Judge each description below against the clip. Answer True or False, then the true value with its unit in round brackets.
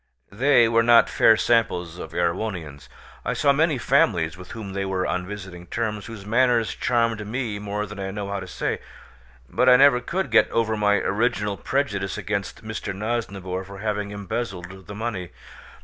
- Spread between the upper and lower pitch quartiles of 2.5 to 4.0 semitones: True (3.3 semitones)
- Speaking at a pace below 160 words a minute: False (175 wpm)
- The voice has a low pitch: True (105 Hz)